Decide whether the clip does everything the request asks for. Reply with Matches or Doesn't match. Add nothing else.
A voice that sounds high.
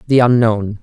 Doesn't match